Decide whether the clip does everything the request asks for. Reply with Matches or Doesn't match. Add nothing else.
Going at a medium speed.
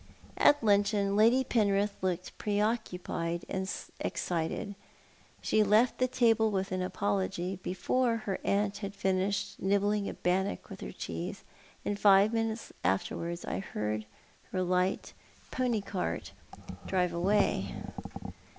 Doesn't match